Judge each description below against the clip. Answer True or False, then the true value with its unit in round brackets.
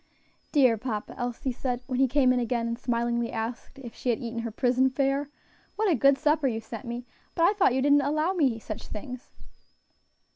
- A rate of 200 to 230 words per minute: True (205 wpm)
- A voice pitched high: True (250 Hz)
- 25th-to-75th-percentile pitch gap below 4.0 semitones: True (2.9 semitones)